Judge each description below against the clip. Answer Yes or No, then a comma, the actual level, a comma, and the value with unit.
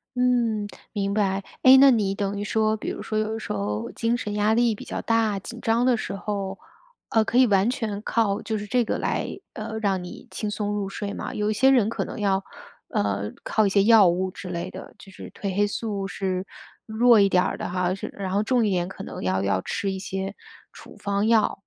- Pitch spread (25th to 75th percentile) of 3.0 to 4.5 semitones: No, narrow, 2.5 semitones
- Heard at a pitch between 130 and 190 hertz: No, high, 205 Hz